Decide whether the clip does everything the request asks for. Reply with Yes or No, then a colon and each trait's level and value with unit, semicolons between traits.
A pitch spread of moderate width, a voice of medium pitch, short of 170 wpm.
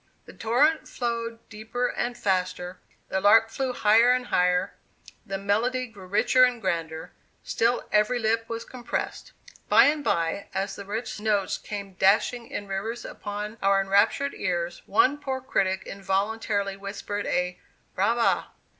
No: average, 3.6 semitones; high, 210 Hz; average, 145 wpm